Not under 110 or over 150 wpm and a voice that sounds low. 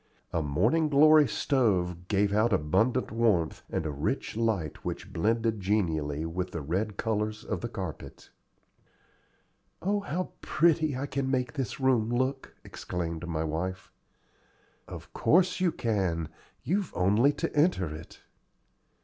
Yes: slow, 135 wpm; low, 110 Hz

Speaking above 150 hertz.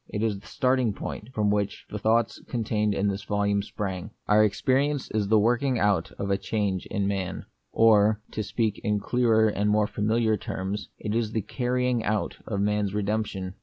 No: low, 105 Hz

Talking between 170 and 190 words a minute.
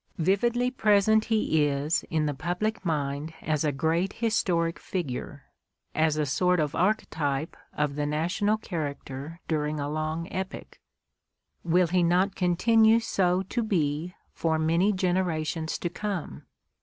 No: average, 140 wpm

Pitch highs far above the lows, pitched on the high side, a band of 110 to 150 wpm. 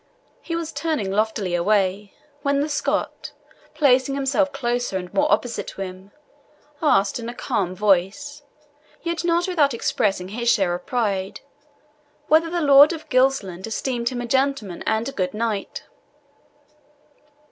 Yes: wide, 6.4 semitones; high, 240 Hz; average, 145 wpm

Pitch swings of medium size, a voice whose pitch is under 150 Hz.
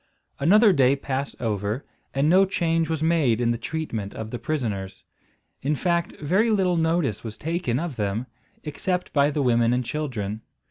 No: wide, 6.1 semitones; medium, 140 Hz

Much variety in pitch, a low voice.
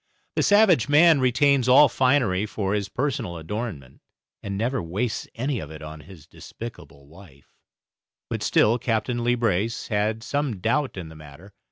Yes: wide, 6.0 semitones; low, 110 Hz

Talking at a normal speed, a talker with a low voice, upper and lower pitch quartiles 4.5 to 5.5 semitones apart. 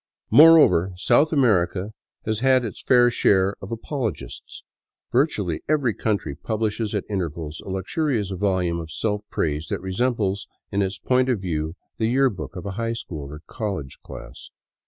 Yes: average, 155 wpm; low, 100 Hz; average, 4.8 semitones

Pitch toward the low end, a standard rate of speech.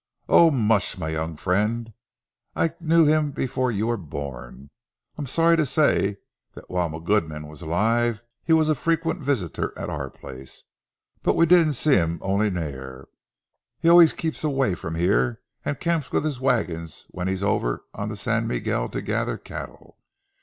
Yes: low, 110 Hz; average, 170 wpm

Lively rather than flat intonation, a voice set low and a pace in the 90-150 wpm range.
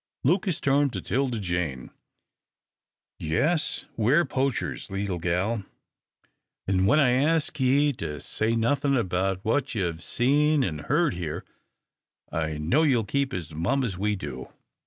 Yes: wide, 7.7 semitones; low, 115 Hz; slow, 135 wpm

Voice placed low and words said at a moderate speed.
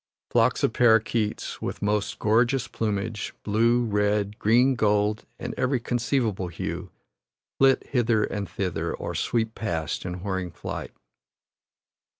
No: low, 110 Hz; slow, 125 wpm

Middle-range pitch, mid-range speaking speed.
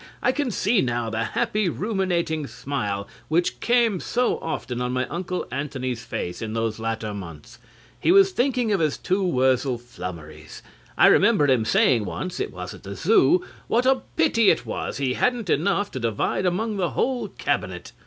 Yes: medium, 150 Hz; average, 175 wpm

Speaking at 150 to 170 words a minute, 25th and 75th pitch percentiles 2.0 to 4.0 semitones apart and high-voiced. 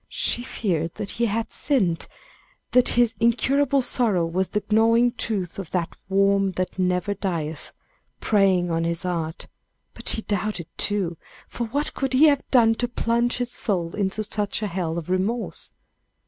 No: average, 160 wpm; average, 4.7 semitones; high, 205 Hz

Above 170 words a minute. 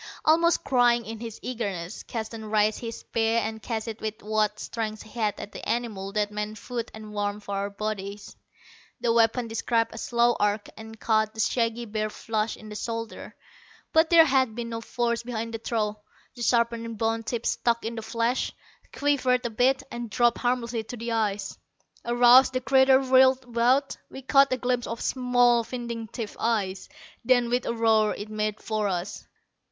Yes: average, 180 wpm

